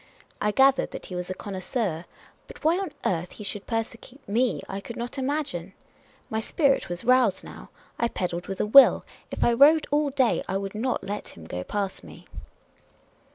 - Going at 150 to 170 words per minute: No, average, 190 wpm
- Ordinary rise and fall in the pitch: No, wide, 5.8 semitones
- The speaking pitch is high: Yes, high, 225 Hz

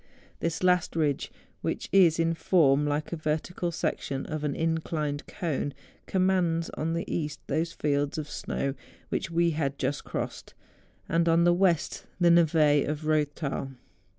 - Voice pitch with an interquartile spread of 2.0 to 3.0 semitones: Yes, narrow, 2.4 semitones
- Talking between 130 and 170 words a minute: Yes, average, 160 wpm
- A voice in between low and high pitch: Yes, medium, 160 Hz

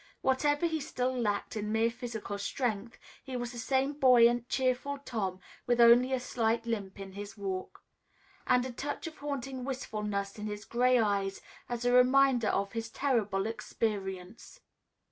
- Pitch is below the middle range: No, high, 235 Hz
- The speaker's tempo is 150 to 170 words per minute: Yes, average, 160 wpm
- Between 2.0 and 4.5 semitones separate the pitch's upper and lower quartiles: Yes, average, 3.7 semitones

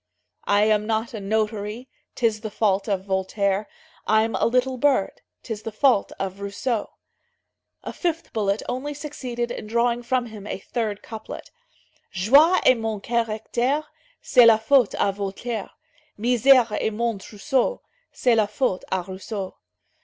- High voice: Yes, high, 220 Hz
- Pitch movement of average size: Yes, average, 3.2 semitones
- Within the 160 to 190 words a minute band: No, average, 145 wpm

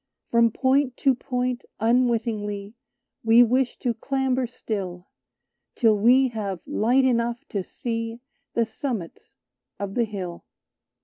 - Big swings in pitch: No, average, 3.0 semitones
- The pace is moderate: No, slow, 120 wpm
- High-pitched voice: Yes, high, 235 Hz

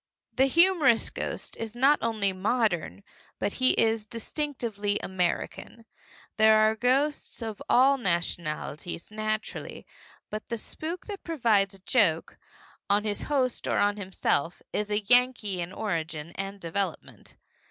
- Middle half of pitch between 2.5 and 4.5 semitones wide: Yes, average, 4.2 semitones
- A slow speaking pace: Yes, slow, 130 wpm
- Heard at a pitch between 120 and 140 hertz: No, high, 215 Hz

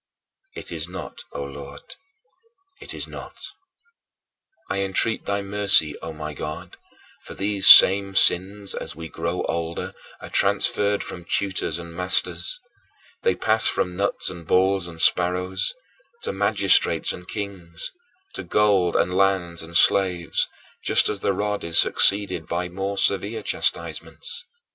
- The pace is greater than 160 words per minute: No, average, 140 wpm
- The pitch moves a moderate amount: Yes, average, 3.0 semitones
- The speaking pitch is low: Yes, very low, 95 Hz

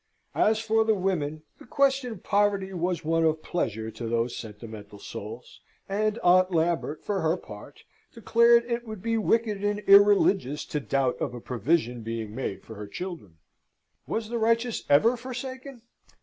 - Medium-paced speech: Yes, average, 165 wpm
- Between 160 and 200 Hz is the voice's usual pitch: Yes, medium, 185 Hz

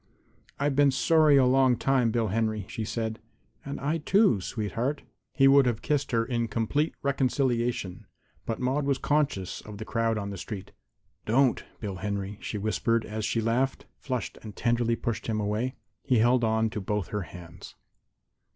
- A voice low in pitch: Yes, low, 115 Hz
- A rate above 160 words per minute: Yes, average, 170 wpm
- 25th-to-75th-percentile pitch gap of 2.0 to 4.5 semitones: Yes, average, 3.9 semitones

